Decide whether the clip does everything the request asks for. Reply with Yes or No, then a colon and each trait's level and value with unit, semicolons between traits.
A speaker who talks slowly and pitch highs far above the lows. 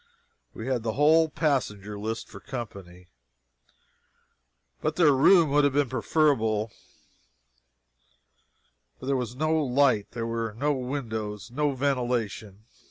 No: slow, 120 wpm; average, 4.6 semitones